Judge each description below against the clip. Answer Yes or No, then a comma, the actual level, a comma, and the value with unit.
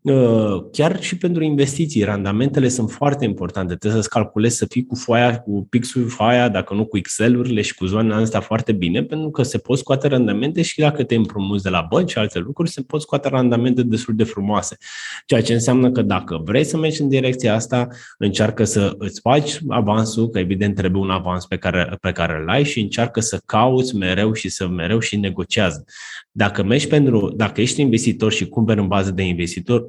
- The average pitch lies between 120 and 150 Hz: No, low, 110 Hz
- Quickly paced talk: Yes, fast, 200 wpm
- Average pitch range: Yes, average, 4.1 semitones